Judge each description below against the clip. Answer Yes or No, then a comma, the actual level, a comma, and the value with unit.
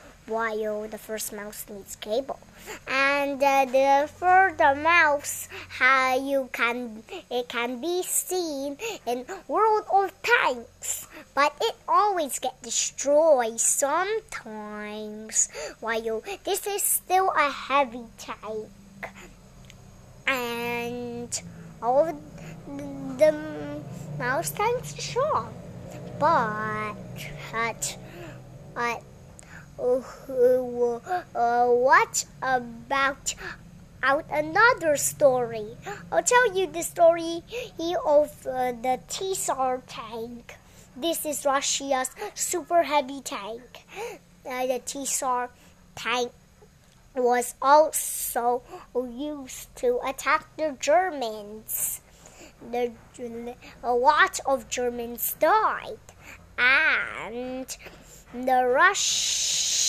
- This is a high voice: Yes, very high, 265 Hz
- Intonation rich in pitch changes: Yes, wide, 5.8 semitones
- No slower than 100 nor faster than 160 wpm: No, average, 90 wpm